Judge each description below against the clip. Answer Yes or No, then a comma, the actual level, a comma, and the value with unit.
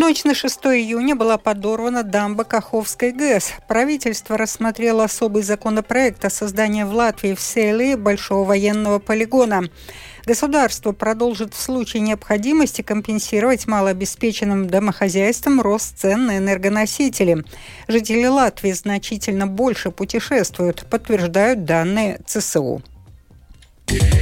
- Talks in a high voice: Yes, high, 220 Hz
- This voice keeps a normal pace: No, slow, 105 wpm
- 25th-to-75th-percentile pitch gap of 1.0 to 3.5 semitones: Yes, average, 2.8 semitones